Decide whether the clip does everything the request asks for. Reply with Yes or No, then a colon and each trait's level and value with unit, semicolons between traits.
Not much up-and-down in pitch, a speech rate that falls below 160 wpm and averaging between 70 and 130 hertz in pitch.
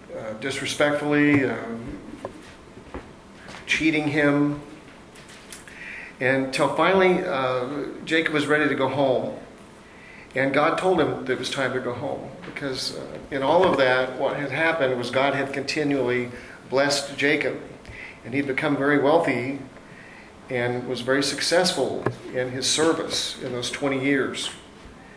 No: narrow, 2.3 semitones; slow, 135 wpm; medium, 140 Hz